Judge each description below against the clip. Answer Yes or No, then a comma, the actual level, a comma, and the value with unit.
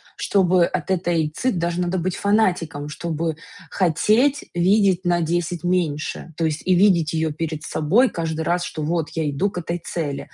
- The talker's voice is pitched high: No, medium, 170 Hz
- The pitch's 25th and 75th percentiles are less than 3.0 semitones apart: Yes, narrow, 2.6 semitones